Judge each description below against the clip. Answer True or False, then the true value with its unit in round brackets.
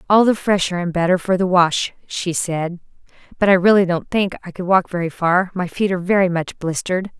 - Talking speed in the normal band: False (215 wpm)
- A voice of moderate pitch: True (180 Hz)